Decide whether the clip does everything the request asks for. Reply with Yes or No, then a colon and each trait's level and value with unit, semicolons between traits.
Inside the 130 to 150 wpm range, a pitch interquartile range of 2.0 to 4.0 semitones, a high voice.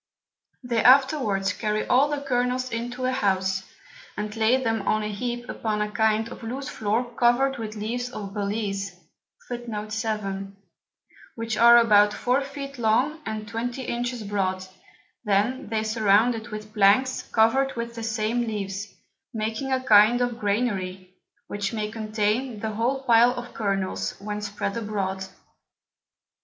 Yes: average, 145 wpm; average, 2.9 semitones; high, 225 Hz